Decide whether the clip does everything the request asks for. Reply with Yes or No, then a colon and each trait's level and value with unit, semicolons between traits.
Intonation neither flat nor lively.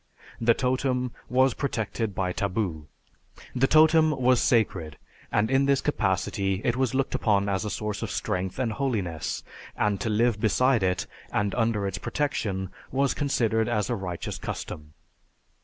Yes: average, 4.8 semitones